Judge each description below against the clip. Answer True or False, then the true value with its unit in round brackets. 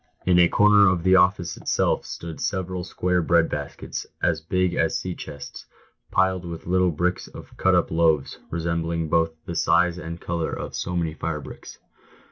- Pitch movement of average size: False (1.8 semitones)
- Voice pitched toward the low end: True (85 Hz)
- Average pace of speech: True (165 wpm)